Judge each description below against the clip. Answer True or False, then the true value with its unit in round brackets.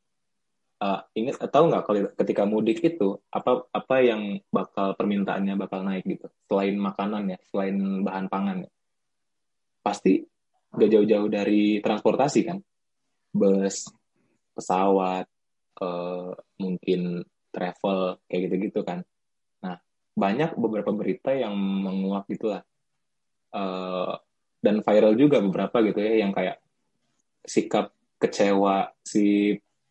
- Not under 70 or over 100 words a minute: False (110 wpm)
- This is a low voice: True (100 Hz)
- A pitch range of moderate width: False (1.7 semitones)